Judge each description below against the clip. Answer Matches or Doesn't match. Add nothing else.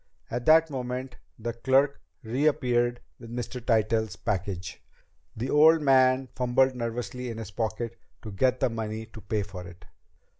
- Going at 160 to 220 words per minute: Doesn't match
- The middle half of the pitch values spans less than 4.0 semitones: Matches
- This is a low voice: Matches